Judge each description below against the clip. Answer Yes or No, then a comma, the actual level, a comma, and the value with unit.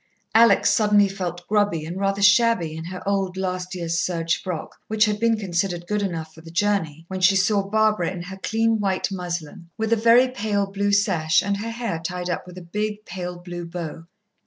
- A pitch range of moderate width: Yes, average, 3.2 semitones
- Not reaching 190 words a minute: No, fast, 205 wpm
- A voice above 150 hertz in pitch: Yes, high, 190 Hz